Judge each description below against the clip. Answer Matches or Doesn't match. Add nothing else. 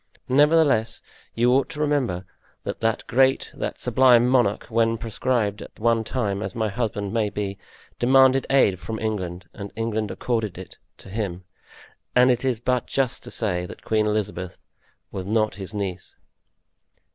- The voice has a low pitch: Matches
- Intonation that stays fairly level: Doesn't match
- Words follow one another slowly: Doesn't match